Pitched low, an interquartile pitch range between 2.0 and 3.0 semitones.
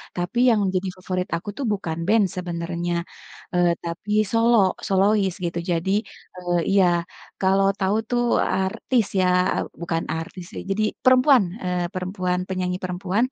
No: medium, 185 Hz; average, 2.7 semitones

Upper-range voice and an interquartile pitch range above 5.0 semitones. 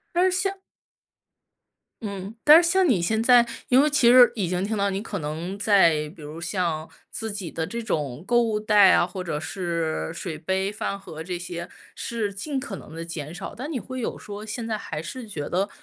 Yes: high, 200 Hz; wide, 5.5 semitones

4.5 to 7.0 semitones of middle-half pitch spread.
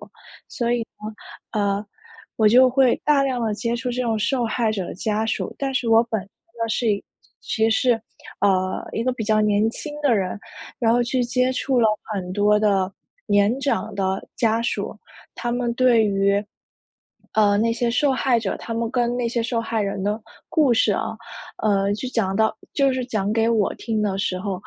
No: average, 3.0 semitones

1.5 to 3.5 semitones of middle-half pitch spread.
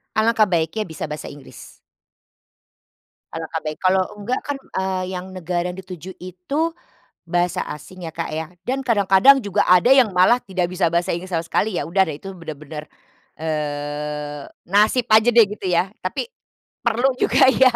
No: average, 4.8 semitones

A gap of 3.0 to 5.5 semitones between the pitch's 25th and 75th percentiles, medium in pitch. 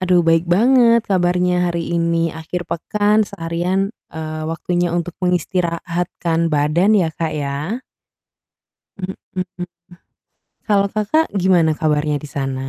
No: narrow, 2.5 semitones; medium, 175 Hz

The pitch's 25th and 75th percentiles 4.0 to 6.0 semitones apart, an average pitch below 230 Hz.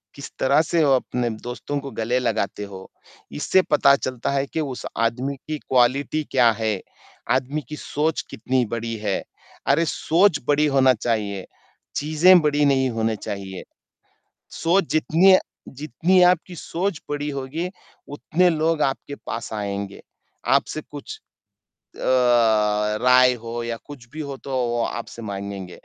Yes: average, 4.7 semitones; low, 135 Hz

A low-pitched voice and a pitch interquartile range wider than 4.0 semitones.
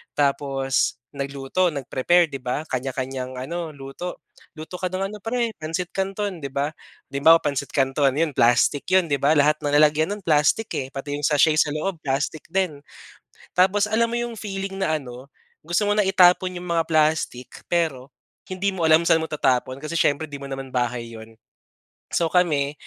No: medium, 155 Hz; average, 4.8 semitones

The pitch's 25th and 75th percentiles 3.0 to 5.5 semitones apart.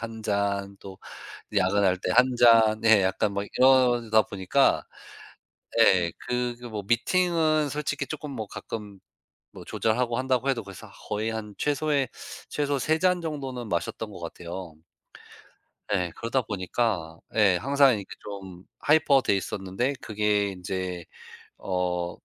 Yes: average, 5.1 semitones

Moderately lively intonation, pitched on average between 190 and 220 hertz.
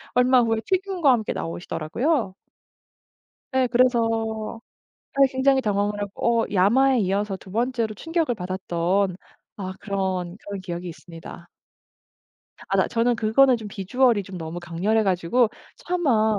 Yes: average, 4.9 semitones; high, 215 Hz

